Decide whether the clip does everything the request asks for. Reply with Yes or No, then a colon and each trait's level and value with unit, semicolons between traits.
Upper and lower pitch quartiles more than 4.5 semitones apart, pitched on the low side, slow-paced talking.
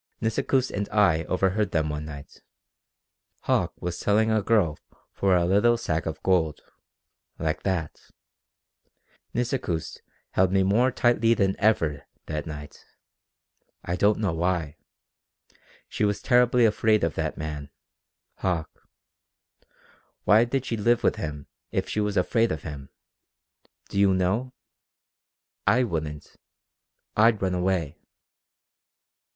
Yes: wide, 5.5 semitones; very low, 95 Hz; slow, 125 wpm